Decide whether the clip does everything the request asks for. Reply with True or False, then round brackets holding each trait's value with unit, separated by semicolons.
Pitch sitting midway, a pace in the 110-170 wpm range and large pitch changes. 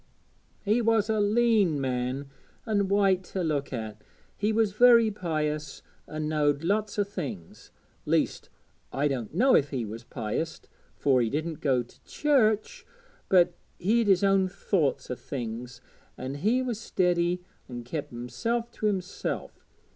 True (175 Hz; 145 wpm; 7.6 semitones)